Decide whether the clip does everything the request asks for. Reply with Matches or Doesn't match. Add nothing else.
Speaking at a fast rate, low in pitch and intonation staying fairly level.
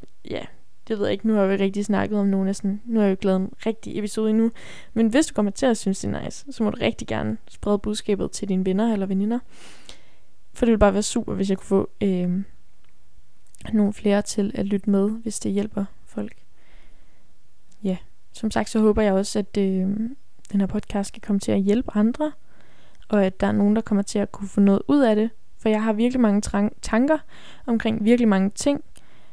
Doesn't match